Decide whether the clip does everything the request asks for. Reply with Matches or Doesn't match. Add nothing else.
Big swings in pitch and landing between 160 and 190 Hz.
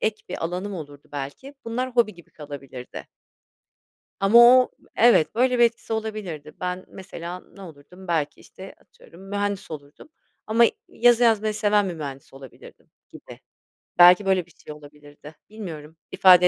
Matches